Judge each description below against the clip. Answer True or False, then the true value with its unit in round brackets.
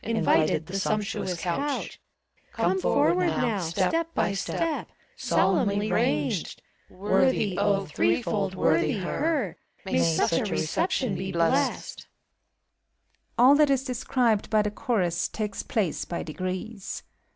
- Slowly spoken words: True (120 wpm)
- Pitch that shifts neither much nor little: True (4.9 semitones)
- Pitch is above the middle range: True (195 Hz)